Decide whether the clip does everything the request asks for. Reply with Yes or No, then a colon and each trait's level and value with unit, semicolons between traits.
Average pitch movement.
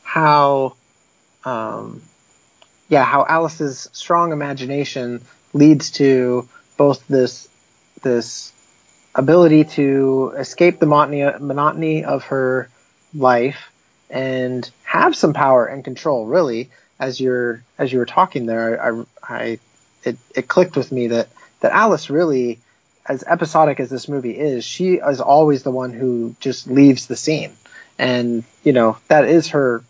Yes: average, 3.1 semitones